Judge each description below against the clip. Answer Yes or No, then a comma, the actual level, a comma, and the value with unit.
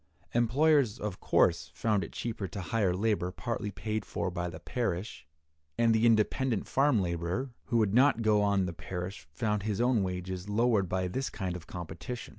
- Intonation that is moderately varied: Yes, average, 4.3 semitones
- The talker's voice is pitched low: Yes, low, 105 Hz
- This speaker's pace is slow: No, average, 180 wpm